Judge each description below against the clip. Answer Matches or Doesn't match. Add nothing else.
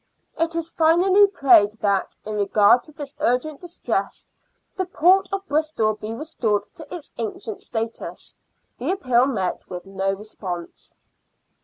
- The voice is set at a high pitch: Matches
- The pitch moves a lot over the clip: Matches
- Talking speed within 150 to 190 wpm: Doesn't match